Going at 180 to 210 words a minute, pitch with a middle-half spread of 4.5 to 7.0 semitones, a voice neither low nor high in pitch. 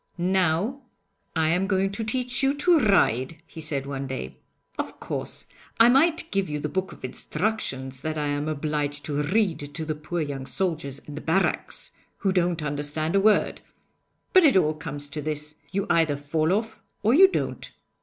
Yes: average, 185 wpm; average, 5.2 semitones; medium, 160 Hz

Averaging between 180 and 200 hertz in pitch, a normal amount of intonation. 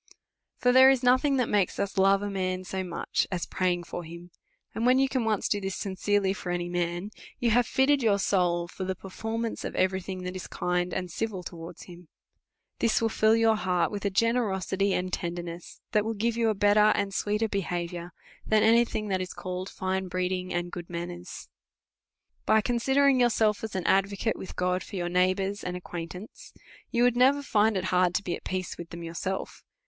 Yes: high, 190 Hz; average, 3.6 semitones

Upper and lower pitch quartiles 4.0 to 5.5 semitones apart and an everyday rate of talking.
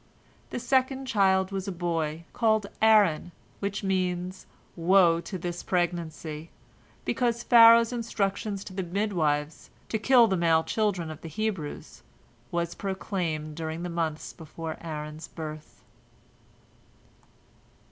No: average, 4.3 semitones; slow, 120 wpm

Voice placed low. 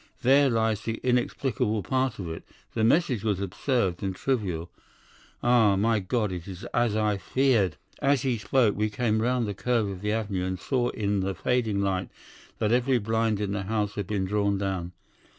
Yes: low, 105 Hz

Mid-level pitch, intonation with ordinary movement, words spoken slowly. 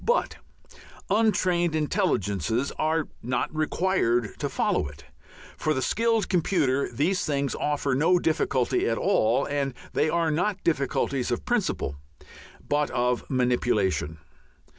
No: medium, 145 Hz; wide, 5.8 semitones; slow, 120 wpm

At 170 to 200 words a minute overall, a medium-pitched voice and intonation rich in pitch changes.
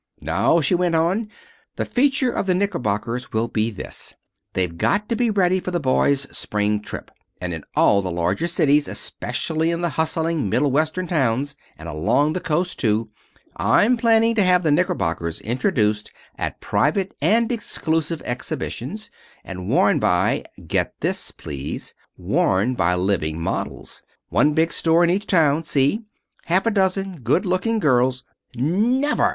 No: average, 155 wpm; medium, 155 Hz; wide, 8.7 semitones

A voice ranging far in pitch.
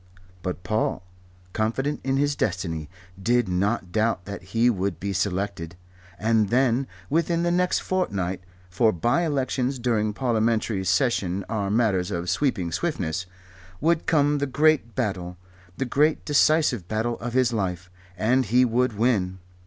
Yes: wide, 5.7 semitones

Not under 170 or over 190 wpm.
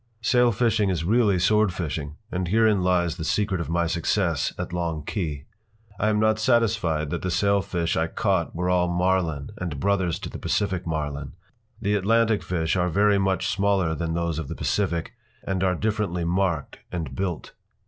Yes: average, 175 wpm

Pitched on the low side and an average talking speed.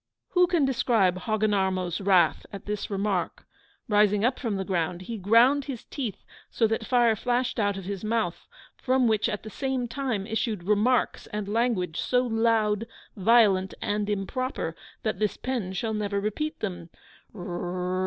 No: high, 215 Hz; average, 155 wpm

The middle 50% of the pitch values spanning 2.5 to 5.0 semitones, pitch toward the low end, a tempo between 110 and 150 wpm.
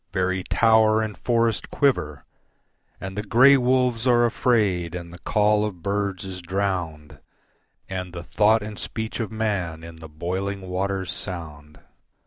Yes: average, 3.9 semitones; low, 100 Hz; average, 145 wpm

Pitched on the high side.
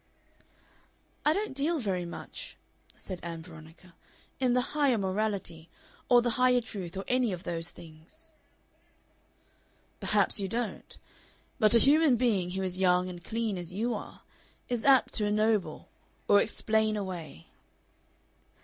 Yes: high, 210 Hz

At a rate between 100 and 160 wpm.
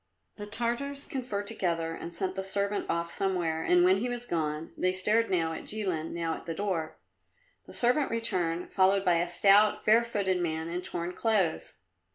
No: average, 185 wpm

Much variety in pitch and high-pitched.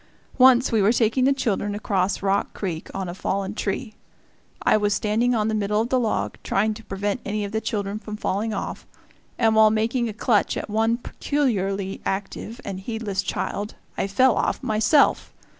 No: narrow, 2.5 semitones; high, 215 Hz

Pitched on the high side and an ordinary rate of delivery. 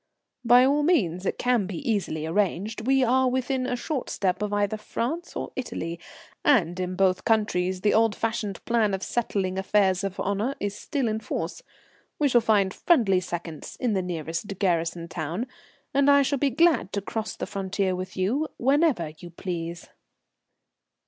Yes: high, 205 Hz; average, 170 wpm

